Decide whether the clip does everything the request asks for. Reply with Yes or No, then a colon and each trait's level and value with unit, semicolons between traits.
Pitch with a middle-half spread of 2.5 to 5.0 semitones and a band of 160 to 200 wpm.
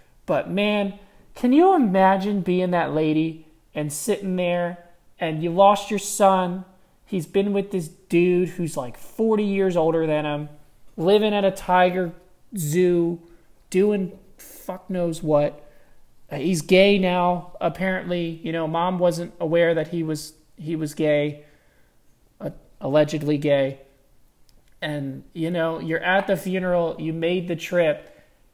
No: average, 3.1 semitones; slow, 135 wpm